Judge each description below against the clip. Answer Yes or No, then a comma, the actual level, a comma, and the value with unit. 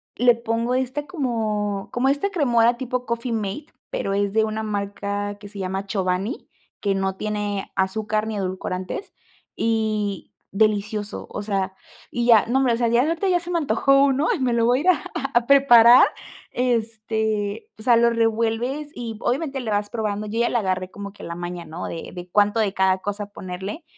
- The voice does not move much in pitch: No, average, 3.3 semitones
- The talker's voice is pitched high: Yes, high, 220 Hz